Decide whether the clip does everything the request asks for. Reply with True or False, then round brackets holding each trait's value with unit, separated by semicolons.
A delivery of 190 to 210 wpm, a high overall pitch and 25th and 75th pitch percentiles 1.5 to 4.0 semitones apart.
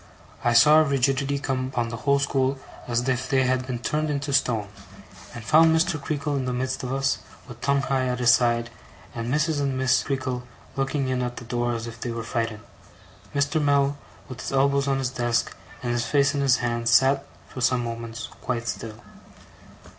False (200 wpm; 130 Hz; 2.6 semitones)